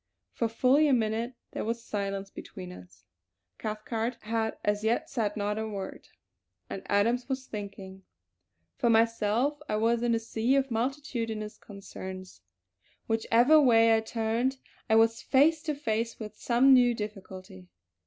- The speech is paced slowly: No, average, 145 wpm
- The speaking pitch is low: No, high, 225 Hz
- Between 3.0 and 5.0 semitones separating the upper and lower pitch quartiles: No, narrow, 2.6 semitones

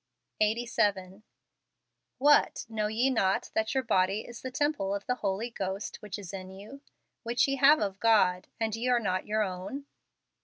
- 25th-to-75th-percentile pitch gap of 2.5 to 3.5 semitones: No, average, 3.9 semitones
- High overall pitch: Yes, high, 215 Hz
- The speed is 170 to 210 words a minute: Yes, average, 180 wpm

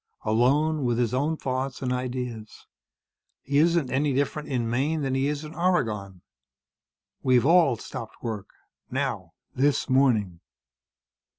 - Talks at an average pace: No, slow, 130 wpm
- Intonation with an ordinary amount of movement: Yes, average, 3.6 semitones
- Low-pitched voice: Yes, low, 130 Hz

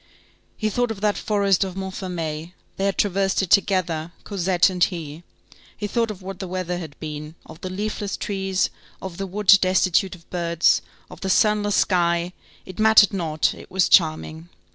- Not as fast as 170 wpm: No, average, 175 wpm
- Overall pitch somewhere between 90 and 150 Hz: No, medium, 185 Hz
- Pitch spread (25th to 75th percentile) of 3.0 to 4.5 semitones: No, narrow, 2.6 semitones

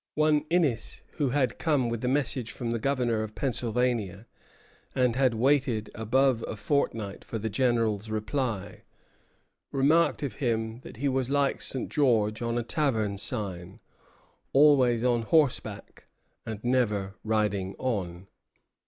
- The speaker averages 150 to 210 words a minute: No, slow, 135 wpm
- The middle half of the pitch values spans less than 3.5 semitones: No, average, 3.8 semitones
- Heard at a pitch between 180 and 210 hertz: No, low, 120 Hz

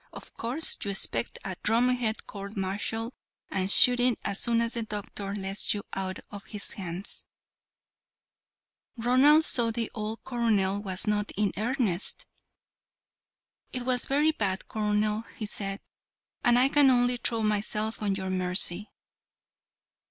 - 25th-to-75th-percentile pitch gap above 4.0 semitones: No, average, 3.4 semitones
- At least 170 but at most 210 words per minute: No, average, 140 wpm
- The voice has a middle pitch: No, high, 215 Hz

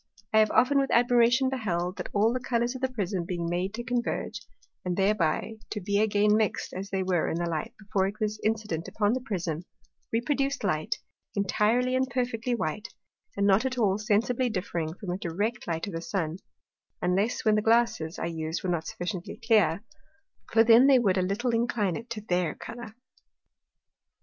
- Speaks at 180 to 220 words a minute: Yes, average, 190 wpm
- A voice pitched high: Yes, high, 210 Hz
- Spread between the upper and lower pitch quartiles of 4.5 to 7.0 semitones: Yes, average, 4.8 semitones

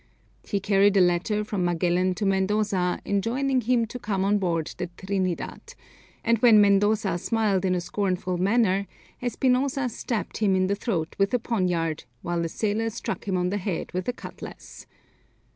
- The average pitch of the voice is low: No, high, 200 Hz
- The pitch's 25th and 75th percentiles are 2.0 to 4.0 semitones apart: Yes, average, 3.2 semitones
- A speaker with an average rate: Yes, average, 170 wpm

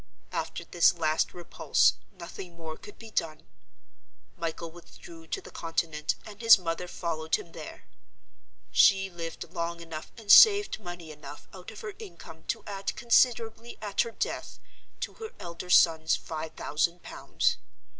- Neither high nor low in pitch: Yes, medium, 170 Hz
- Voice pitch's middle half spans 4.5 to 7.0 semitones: No, average, 3.9 semitones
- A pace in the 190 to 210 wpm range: No, average, 150 wpm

